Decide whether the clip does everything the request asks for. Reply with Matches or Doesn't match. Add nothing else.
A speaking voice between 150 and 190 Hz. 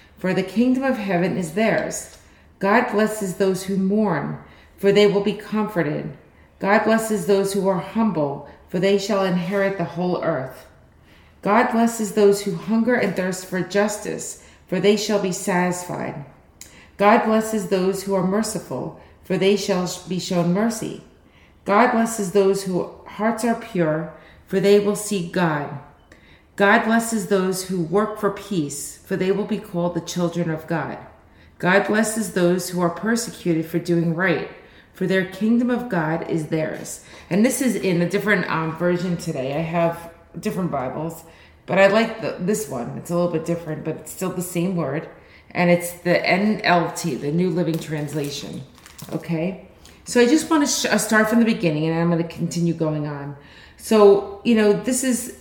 Matches